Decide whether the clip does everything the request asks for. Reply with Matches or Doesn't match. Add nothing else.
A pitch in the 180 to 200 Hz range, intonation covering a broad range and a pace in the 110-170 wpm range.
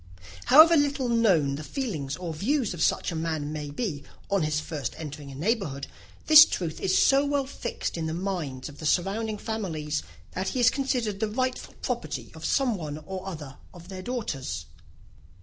Doesn't match